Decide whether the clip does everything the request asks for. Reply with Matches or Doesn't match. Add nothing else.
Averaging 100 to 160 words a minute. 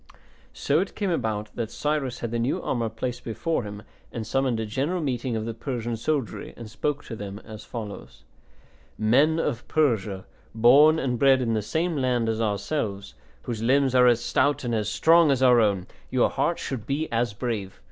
Doesn't match